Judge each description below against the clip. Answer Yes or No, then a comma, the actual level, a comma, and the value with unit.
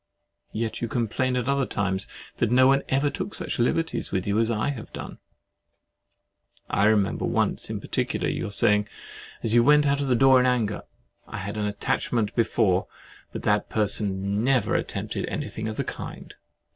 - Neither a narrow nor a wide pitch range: Yes, average, 3.8 semitones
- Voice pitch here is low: Yes, low, 115 Hz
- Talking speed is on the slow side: No, average, 170 wpm